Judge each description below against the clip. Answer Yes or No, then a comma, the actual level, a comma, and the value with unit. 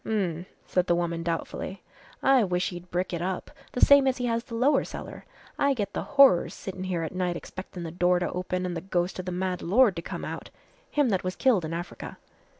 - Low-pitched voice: No, medium, 185 Hz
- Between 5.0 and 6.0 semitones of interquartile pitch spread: No, average, 4.2 semitones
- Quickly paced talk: Yes, fast, 230 wpm